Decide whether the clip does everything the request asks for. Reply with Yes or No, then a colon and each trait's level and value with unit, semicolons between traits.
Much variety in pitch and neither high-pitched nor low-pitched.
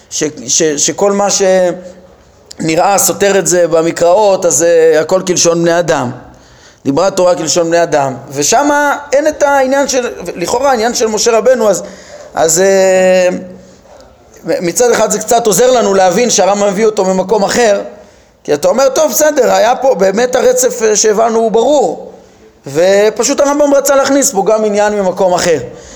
No: wide, 6.0 semitones; high, 200 Hz